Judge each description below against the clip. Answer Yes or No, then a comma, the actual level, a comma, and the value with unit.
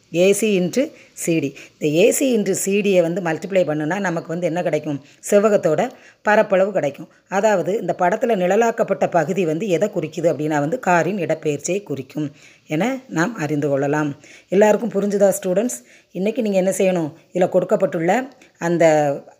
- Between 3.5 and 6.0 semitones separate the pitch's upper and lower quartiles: Yes, average, 4.5 semitones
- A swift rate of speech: Yes, fast, 135 wpm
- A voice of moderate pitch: Yes, medium, 180 Hz